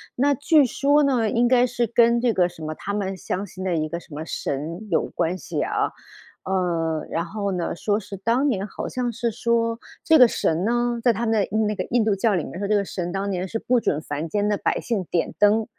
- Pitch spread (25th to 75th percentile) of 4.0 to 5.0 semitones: Yes, average, 4.7 semitones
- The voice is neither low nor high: No, high, 205 Hz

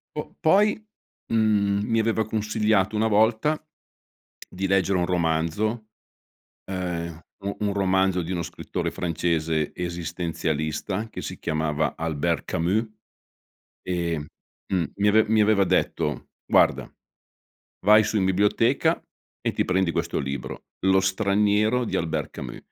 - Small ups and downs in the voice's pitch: No, average, 4.2 semitones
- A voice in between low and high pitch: No, very low, 95 Hz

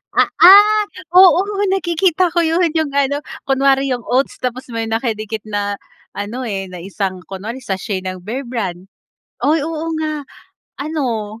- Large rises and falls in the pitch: Yes, wide, 7.2 semitones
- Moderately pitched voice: No, very high, 255 Hz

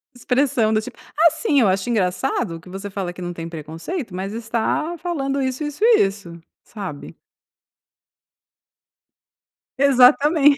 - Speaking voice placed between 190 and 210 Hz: No, high, 230 Hz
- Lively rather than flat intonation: Yes, wide, 7.0 semitones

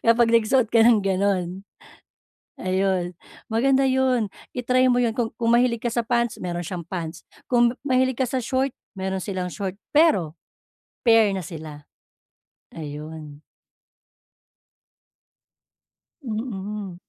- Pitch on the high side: Yes, high, 220 Hz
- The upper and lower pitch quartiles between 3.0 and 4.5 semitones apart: No, average, 4.9 semitones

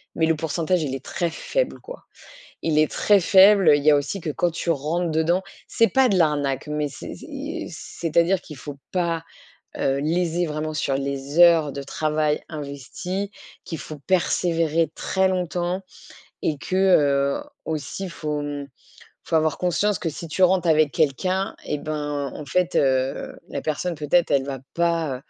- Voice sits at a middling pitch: Yes, medium, 160 Hz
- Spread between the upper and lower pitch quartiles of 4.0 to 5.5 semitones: No, average, 3.5 semitones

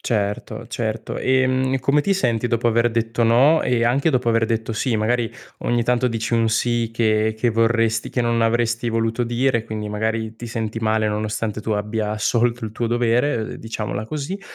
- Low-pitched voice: Yes, low, 115 Hz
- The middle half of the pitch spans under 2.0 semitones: Yes, narrow, 1.5 semitones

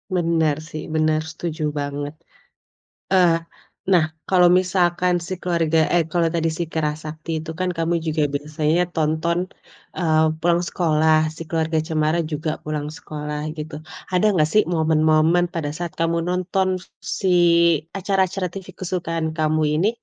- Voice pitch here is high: No, medium, 165 Hz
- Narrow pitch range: Yes, narrow, 2.1 semitones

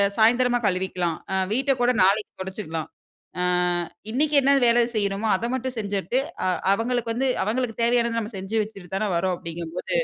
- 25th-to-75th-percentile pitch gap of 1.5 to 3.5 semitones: No, average, 4.3 semitones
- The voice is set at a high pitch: Yes, high, 220 Hz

